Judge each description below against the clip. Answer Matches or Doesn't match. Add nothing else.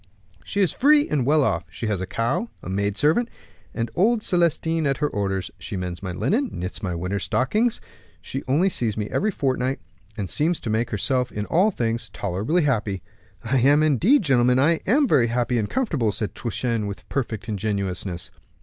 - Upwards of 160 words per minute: Matches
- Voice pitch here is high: Doesn't match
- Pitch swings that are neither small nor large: Doesn't match